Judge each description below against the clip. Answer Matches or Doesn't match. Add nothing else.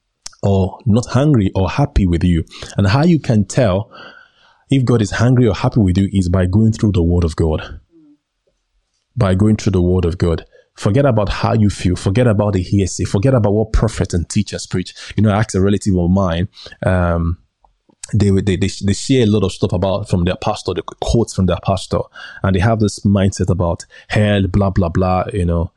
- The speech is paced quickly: Matches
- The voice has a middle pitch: Doesn't match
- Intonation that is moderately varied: Matches